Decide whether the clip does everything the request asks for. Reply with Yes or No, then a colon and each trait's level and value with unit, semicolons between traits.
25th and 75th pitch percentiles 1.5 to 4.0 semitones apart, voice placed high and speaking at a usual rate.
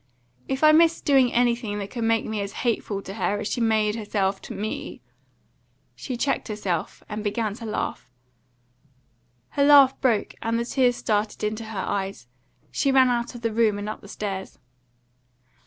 Yes: average, 2.9 semitones; high, 220 Hz; average, 180 wpm